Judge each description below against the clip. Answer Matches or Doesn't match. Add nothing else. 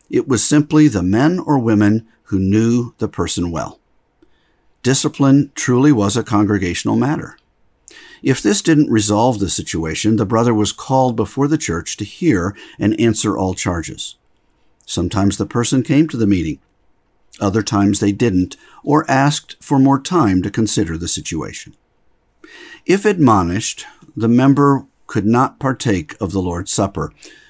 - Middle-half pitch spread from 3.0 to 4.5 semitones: Doesn't match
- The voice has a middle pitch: Doesn't match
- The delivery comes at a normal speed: Matches